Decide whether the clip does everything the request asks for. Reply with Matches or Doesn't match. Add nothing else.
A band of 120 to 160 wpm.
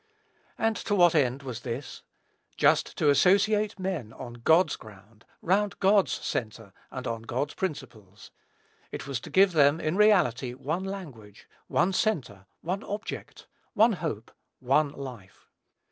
Matches